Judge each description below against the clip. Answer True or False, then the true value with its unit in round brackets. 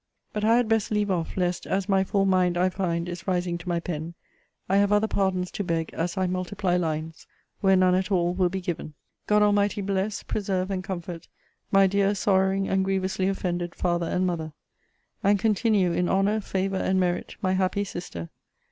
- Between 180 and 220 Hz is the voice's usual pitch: True (185 Hz)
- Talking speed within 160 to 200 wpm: True (190 wpm)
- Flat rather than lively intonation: True (1.8 semitones)